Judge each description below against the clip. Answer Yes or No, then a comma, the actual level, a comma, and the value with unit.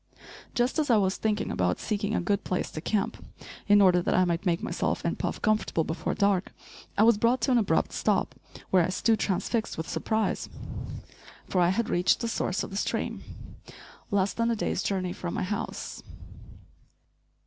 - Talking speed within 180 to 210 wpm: Yes, average, 185 wpm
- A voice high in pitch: Yes, high, 200 Hz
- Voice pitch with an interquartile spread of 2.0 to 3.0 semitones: No, average, 3.4 semitones